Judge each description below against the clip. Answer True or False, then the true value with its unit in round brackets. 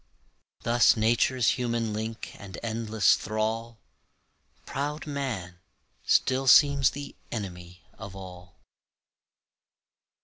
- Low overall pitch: True (115 Hz)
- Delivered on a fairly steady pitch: False (4.5 semitones)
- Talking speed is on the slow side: True (90 wpm)